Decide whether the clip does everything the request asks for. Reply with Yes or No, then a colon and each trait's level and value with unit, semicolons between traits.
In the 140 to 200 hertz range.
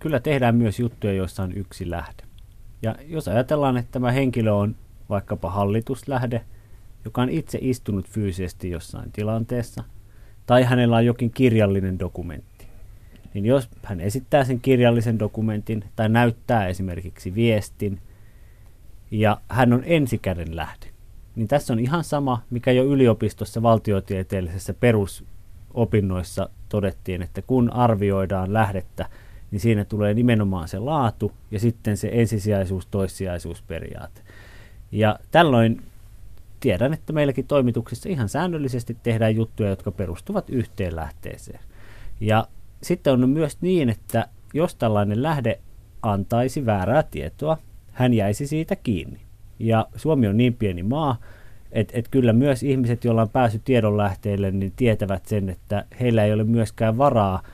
No: low, 110 Hz